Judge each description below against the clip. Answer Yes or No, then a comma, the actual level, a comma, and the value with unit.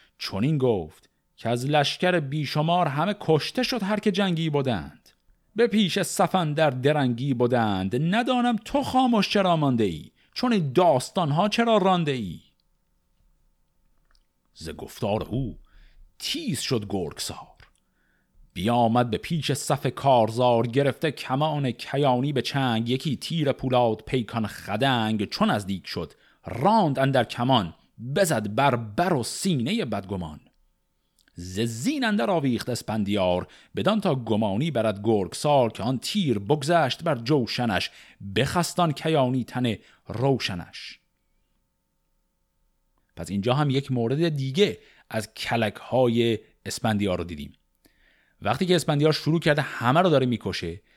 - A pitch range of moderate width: No, wide, 6.7 semitones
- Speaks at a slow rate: No, average, 125 wpm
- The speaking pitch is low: Yes, low, 130 Hz